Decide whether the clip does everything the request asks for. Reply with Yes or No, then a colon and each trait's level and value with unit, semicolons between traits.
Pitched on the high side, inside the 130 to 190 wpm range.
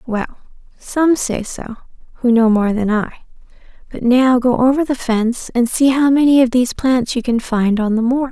No: high, 245 Hz; average, 200 wpm